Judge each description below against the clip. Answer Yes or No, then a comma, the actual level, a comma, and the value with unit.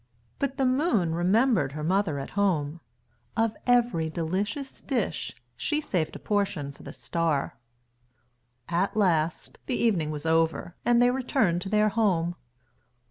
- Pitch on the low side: No, high, 190 Hz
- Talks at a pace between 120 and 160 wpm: Yes, average, 140 wpm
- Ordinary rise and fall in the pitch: No, wide, 6.4 semitones